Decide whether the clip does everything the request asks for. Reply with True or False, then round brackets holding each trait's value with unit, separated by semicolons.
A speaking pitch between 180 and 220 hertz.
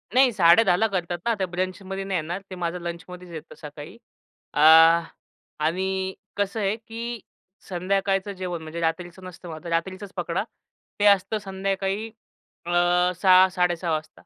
True (185 Hz)